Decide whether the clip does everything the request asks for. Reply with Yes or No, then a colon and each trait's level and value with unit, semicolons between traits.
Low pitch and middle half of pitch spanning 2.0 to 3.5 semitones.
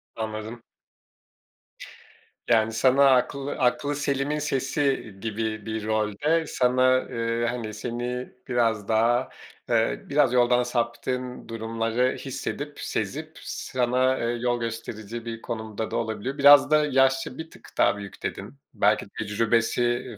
Yes: low, 120 Hz; average, 2.8 semitones